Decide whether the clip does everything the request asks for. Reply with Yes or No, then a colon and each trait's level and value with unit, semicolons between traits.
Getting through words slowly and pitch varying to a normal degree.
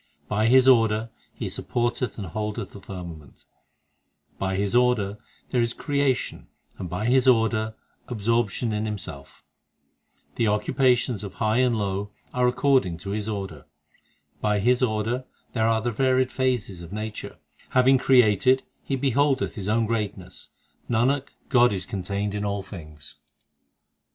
No: average, 150 wpm; average, 3.7 semitones